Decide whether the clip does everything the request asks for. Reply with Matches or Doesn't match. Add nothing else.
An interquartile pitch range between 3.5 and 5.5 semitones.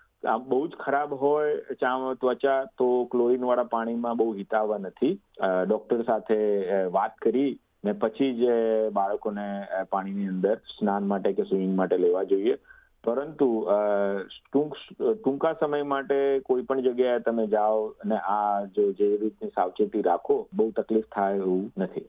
Matches